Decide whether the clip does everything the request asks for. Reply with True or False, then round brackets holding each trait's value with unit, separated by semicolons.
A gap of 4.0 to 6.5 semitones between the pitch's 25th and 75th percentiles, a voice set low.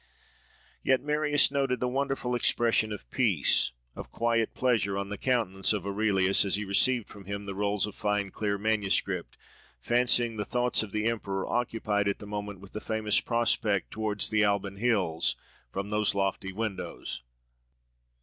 False (2.9 semitones; 105 Hz)